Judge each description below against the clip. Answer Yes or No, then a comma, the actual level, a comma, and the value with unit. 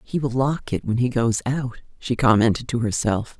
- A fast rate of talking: Yes, fast, 210 wpm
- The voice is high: No, low, 120 Hz